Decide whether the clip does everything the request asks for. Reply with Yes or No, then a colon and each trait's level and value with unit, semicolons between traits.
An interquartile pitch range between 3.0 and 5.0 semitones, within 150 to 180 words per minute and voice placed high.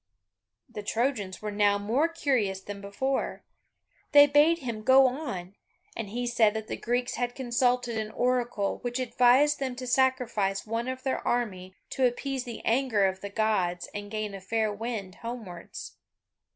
Yes: average, 3.9 semitones; average, 165 wpm; high, 235 Hz